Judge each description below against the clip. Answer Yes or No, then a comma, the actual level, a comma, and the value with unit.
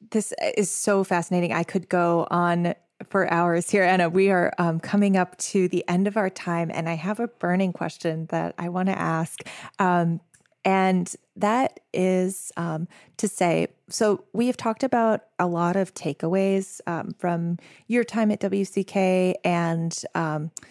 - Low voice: No, medium, 185 Hz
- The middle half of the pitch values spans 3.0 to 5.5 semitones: No, narrow, 2.6 semitones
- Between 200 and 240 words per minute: No, average, 170 wpm